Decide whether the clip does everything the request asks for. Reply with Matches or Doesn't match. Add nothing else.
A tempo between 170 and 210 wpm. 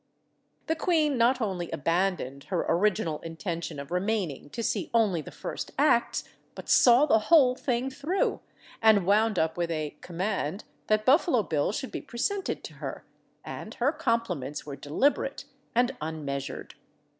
Doesn't match